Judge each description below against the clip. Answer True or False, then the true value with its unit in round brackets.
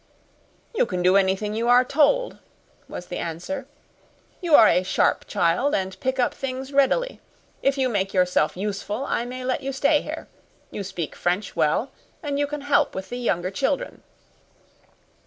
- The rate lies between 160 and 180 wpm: True (170 wpm)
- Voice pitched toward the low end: False (245 Hz)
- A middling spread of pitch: False (6.7 semitones)